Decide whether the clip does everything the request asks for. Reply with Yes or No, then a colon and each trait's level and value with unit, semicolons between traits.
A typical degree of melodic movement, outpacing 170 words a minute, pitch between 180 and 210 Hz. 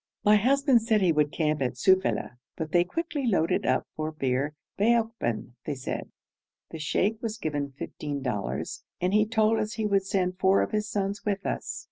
No: wide, 6.2 semitones; average, 185 wpm; high, 190 Hz